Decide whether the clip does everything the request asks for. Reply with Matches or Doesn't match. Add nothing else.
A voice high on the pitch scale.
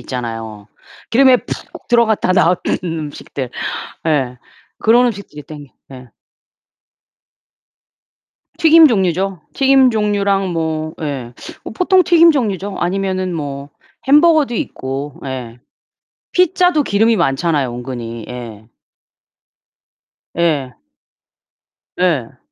Doesn't match